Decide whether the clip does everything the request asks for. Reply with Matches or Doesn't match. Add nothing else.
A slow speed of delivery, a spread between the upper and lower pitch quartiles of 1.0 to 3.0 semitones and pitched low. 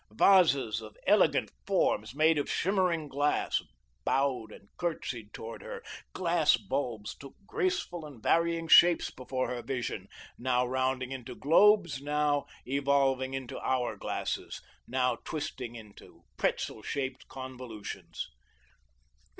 Doesn't match